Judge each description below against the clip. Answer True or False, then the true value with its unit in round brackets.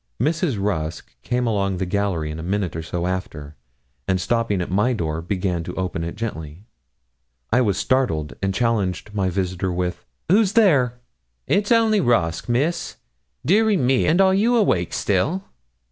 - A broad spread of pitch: True (7.0 semitones)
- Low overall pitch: True (100 Hz)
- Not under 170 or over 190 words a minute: False (160 wpm)